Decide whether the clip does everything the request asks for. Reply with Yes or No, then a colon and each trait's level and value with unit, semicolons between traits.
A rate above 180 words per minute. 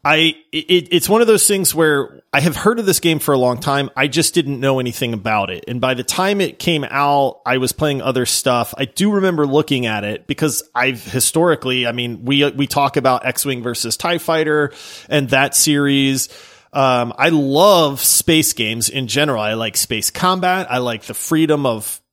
Yes: fast, 205 wpm